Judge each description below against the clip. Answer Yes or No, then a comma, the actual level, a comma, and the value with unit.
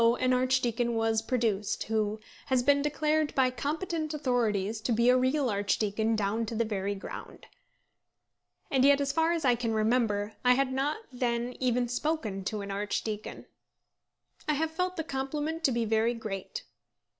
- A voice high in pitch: Yes, high, 245 Hz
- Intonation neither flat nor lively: Yes, average, 4.3 semitones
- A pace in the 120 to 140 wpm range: No, average, 165 wpm